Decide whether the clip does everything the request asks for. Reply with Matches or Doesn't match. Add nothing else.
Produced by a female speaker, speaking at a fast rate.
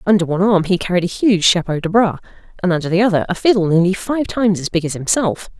Matches